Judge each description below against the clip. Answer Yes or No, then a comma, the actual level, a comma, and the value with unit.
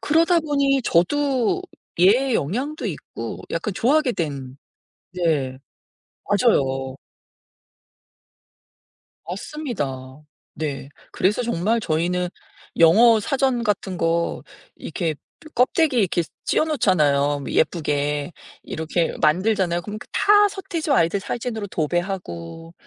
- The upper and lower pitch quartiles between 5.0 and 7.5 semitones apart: No, wide, 8.2 semitones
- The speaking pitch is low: No, medium, 185 Hz